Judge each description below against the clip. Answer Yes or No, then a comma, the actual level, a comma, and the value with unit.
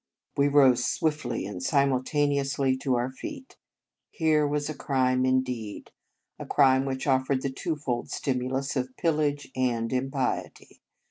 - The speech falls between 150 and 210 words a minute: No, average, 140 wpm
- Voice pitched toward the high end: No, low, 135 Hz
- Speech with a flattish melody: Yes, narrow, 2.2 semitones